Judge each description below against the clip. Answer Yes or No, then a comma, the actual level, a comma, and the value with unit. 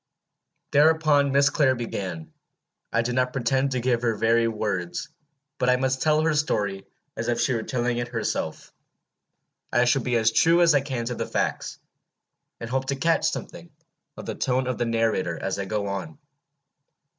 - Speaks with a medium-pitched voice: No, low, 125 Hz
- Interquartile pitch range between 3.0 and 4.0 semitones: Yes, average, 3.3 semitones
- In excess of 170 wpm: Yes, average, 180 wpm